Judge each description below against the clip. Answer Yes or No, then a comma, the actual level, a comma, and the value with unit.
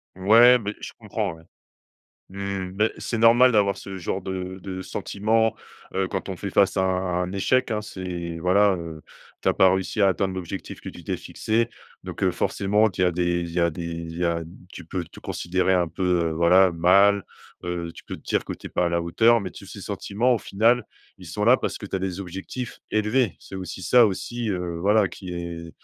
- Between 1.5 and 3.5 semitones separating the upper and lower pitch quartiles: Yes, average, 2.9 semitones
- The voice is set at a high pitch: No, very low, 95 Hz